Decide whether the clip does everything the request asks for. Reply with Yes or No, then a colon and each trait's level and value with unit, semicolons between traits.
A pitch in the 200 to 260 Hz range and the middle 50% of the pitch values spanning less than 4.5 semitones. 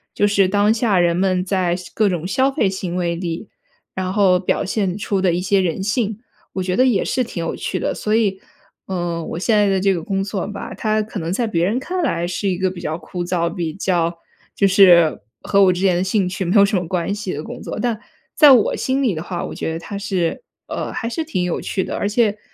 No: high, 190 Hz; average, 2.9 semitones